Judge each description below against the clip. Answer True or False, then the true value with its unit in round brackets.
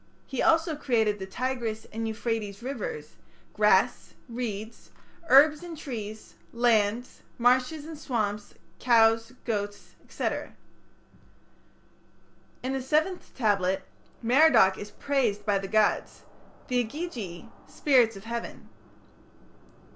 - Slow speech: True (105 wpm)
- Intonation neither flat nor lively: True (4.3 semitones)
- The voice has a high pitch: True (235 Hz)